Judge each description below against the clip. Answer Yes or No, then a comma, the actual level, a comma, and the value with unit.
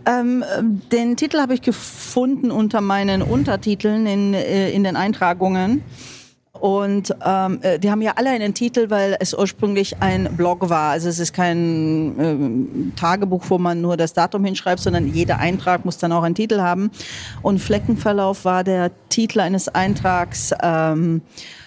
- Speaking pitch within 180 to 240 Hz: Yes, high, 190 Hz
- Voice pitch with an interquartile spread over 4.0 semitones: No, average, 3.7 semitones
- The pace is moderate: Yes, average, 155 wpm